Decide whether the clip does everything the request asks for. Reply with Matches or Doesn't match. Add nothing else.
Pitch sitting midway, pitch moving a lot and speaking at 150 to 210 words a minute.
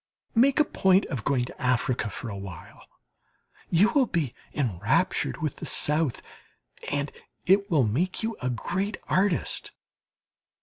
Doesn't match